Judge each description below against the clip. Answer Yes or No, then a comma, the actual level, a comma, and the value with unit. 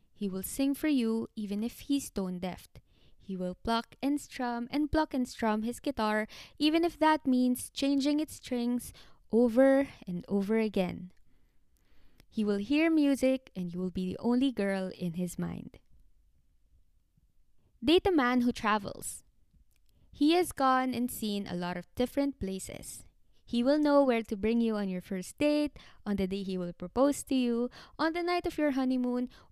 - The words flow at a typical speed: No, fast, 175 wpm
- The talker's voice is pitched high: Yes, high, 240 Hz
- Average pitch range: No, wide, 6.0 semitones